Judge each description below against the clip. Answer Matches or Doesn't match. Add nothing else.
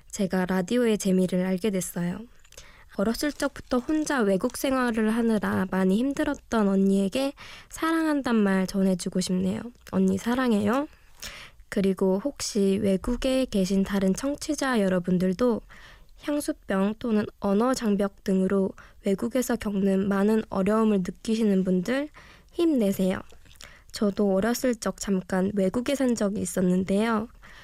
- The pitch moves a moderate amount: Matches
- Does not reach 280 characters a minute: Doesn't match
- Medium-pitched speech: Doesn't match